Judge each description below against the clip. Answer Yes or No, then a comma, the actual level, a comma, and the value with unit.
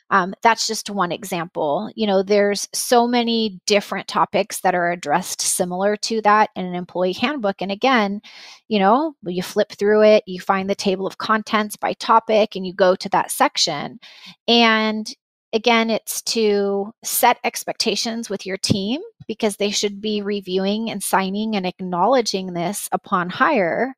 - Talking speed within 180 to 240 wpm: No, average, 165 wpm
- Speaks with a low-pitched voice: No, high, 205 Hz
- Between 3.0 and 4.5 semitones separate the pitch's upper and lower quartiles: No, narrow, 2.6 semitones